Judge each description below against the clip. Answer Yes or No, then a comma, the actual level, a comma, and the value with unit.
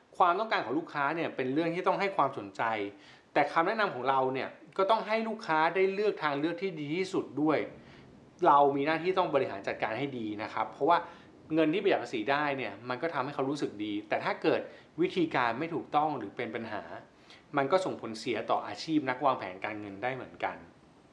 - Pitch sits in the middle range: Yes, medium, 155 Hz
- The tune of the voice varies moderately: No, wide, 6.2 semitones